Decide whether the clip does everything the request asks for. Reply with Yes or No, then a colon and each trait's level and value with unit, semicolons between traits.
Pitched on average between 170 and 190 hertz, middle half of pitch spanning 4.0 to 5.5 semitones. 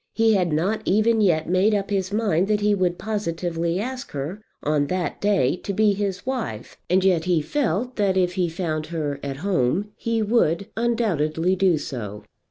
Yes: medium, 185 Hz; average, 4.4 semitones